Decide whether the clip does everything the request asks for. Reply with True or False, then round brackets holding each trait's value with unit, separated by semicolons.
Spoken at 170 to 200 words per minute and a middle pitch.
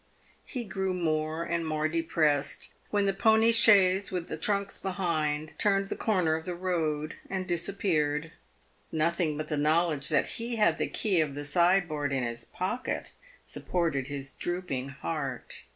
False (155 wpm; 165 Hz)